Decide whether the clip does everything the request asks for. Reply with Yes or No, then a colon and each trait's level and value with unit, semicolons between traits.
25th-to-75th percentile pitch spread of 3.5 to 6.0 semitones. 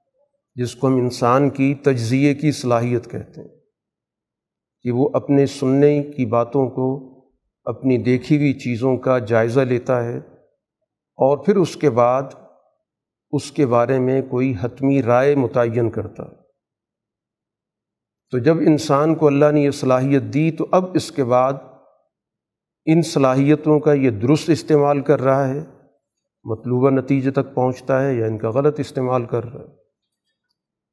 No: average, 2.7 semitones